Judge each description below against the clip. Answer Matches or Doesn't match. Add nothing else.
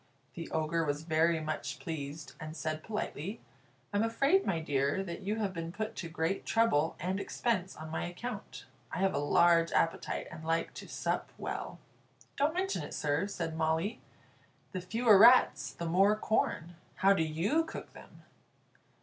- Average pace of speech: Matches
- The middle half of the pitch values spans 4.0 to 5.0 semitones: Matches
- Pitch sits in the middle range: Matches